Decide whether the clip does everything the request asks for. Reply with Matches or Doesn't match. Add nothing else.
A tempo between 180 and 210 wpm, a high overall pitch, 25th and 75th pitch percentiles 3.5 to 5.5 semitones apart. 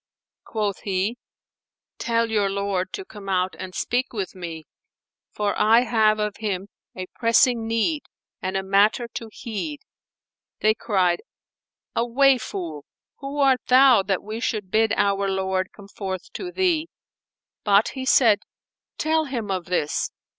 Doesn't match